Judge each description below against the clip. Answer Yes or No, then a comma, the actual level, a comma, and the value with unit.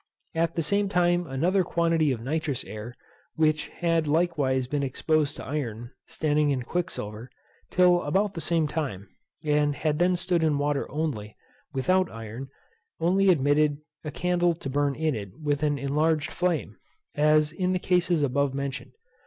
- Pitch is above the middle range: No, medium, 150 Hz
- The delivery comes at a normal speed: Yes, average, 160 wpm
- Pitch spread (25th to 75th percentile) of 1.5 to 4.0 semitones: Yes, average, 3.6 semitones